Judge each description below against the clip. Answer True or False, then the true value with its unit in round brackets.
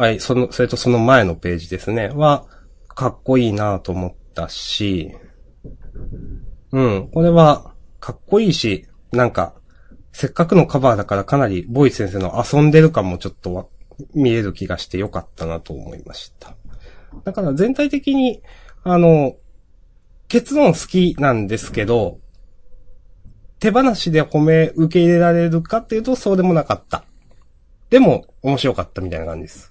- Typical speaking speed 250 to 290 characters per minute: False (305 characters per minute)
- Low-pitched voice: True (120 Hz)